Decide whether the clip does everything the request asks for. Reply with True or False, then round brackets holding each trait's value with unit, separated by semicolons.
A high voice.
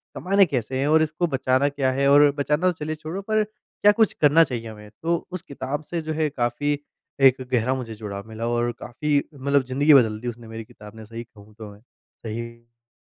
False (130 Hz)